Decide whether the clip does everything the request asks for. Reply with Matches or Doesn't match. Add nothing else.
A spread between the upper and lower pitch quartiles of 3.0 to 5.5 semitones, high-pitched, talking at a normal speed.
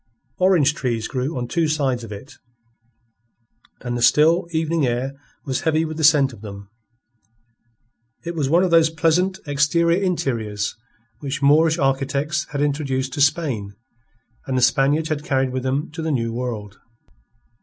Doesn't match